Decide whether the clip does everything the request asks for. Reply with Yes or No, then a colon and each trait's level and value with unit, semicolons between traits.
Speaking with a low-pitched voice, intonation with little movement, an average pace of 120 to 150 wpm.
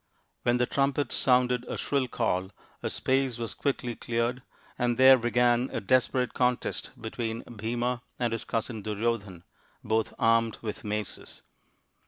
Yes: low, 120 Hz; narrow, 2.0 semitones; average, 140 wpm